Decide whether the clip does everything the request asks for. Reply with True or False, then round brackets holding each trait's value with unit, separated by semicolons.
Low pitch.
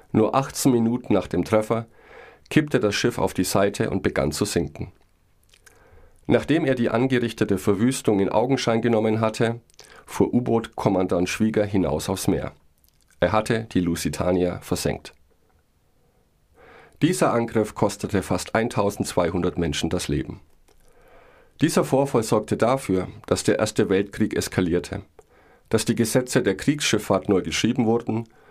True (110 Hz)